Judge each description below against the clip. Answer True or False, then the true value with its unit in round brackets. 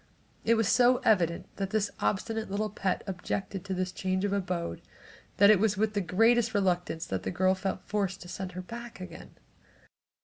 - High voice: True (195 Hz)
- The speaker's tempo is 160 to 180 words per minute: False (190 wpm)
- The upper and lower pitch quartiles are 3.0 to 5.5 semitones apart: False (2.6 semitones)